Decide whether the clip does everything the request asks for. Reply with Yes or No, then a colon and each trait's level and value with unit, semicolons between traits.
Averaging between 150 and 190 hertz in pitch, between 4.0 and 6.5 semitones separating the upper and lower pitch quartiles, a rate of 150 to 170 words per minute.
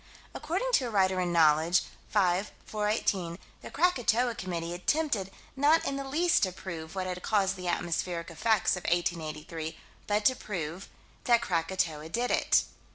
Yes: medium, 185 Hz; average, 5.2 semitones; average, 155 wpm